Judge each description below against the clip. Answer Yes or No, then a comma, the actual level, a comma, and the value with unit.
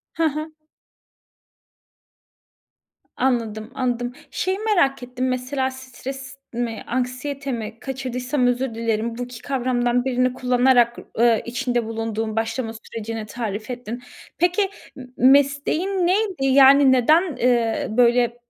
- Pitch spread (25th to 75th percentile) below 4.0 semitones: Yes, narrow, 2.4 semitones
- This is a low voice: No, very high, 250 Hz